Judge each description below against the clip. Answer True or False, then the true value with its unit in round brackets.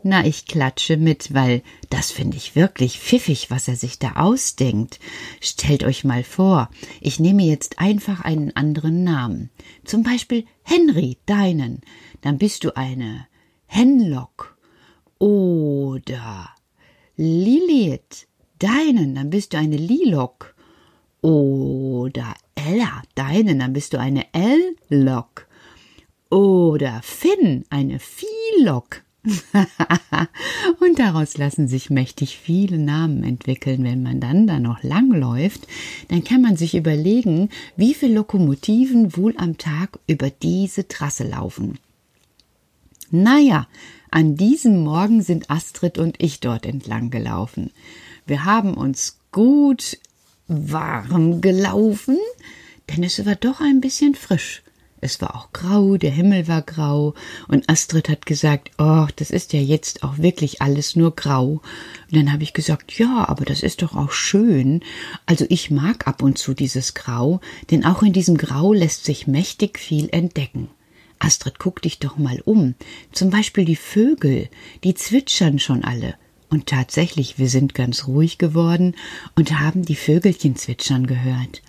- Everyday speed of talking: True (140 wpm)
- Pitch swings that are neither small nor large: False (6.2 semitones)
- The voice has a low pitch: False (160 Hz)